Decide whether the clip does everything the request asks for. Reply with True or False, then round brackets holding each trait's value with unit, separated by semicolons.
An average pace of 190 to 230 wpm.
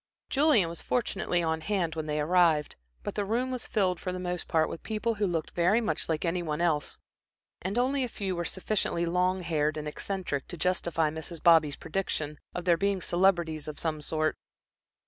True (195 wpm)